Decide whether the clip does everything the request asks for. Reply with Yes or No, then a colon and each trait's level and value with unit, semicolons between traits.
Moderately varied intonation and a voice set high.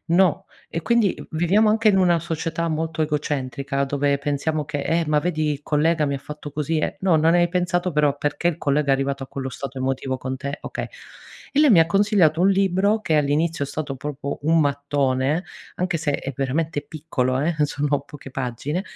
No: average, 3.3 semitones; medium, 150 Hz